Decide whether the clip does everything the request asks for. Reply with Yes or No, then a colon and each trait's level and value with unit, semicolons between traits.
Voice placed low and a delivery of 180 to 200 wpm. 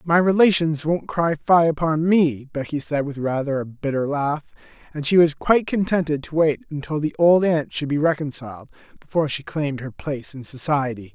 No: medium, 150 Hz; average, 190 wpm